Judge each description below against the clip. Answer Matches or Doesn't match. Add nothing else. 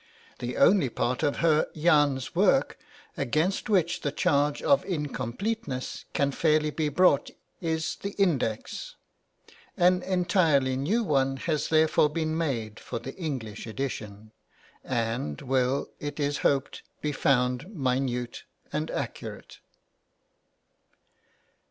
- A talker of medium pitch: Matches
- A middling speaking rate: Doesn't match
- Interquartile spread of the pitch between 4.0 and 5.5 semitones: Matches